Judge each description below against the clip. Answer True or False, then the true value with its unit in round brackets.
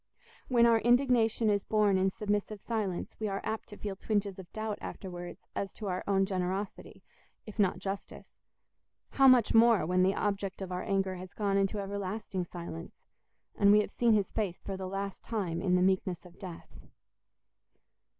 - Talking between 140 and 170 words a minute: False (180 wpm)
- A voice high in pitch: True (195 Hz)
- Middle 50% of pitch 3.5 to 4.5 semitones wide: False (2.4 semitones)